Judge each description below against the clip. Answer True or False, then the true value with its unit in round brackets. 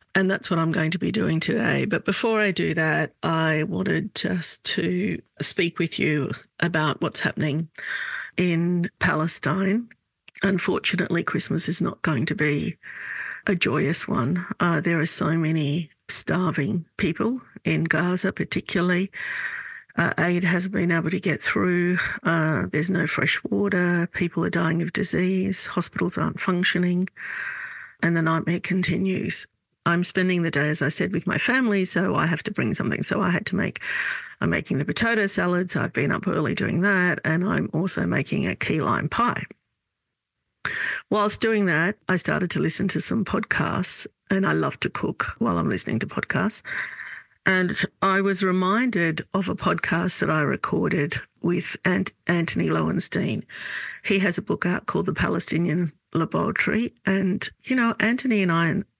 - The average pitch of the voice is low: False (180 Hz)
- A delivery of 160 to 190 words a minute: True (165 wpm)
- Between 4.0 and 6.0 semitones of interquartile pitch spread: False (2.8 semitones)